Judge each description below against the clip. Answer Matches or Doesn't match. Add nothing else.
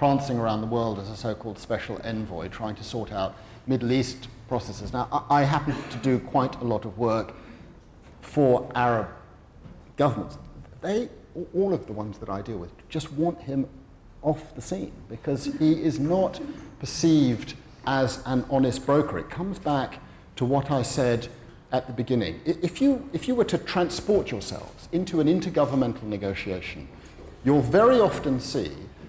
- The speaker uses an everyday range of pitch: Matches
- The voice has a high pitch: Doesn't match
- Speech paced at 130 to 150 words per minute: Doesn't match